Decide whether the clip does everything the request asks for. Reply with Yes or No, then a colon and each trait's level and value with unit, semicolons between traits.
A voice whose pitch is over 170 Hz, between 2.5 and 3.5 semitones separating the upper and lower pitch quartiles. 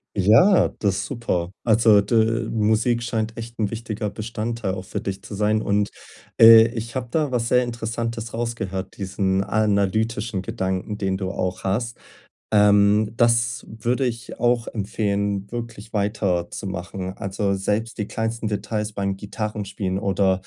No: low, 105 Hz; average, 2.8 semitones